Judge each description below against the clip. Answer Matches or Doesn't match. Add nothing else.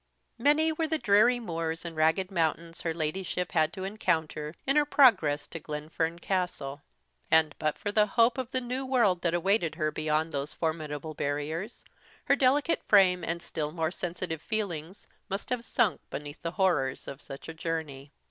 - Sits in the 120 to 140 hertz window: Doesn't match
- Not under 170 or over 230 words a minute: Matches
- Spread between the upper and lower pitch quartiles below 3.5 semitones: Doesn't match